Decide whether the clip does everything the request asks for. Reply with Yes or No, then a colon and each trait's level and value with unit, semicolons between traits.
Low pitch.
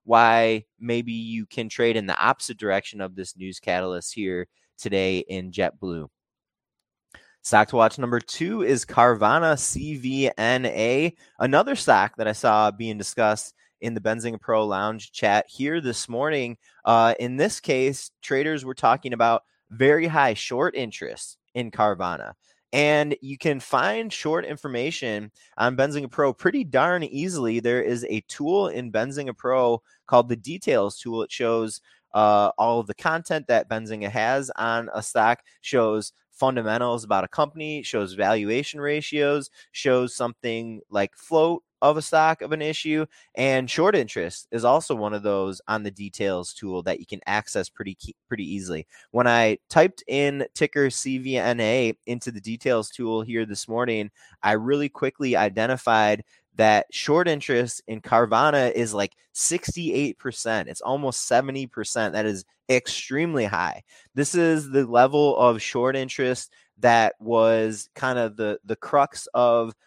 Yes: low, 120 Hz